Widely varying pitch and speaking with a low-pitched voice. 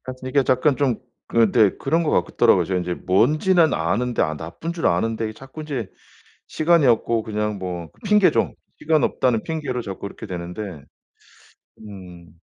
Yes: wide, 7.5 semitones; low, 115 Hz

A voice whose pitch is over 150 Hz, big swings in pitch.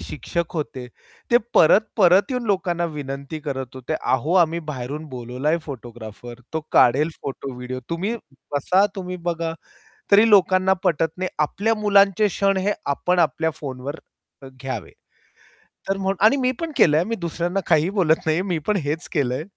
Yes: medium, 165 Hz; wide, 5.7 semitones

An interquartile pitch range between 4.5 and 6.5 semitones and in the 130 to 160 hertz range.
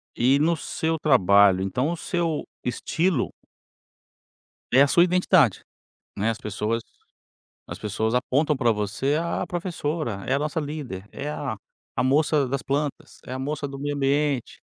Yes: average, 4.8 semitones; medium, 140 Hz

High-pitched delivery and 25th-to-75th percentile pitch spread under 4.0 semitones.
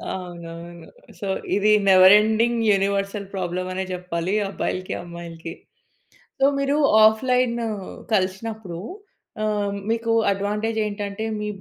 Yes: high, 200 Hz; average, 3.2 semitones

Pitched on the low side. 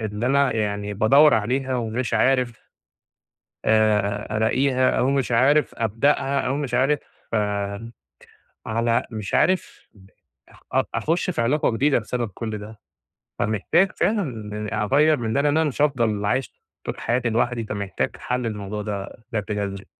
Yes: low, 115 Hz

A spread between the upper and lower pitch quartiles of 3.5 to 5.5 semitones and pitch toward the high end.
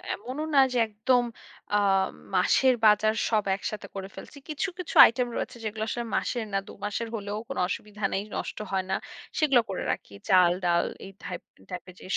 Yes: average, 4.0 semitones; high, 210 Hz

